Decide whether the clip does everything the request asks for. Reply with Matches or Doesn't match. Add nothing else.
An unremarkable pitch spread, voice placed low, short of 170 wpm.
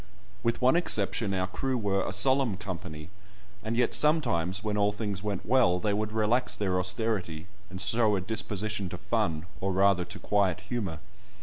Doesn't match